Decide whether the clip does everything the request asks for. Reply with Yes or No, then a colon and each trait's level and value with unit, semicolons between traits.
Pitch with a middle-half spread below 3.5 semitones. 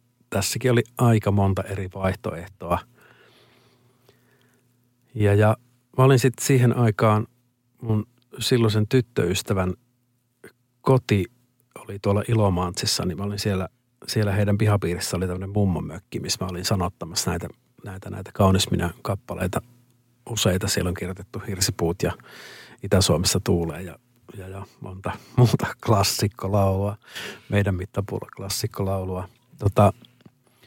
No: average, 4.0 semitones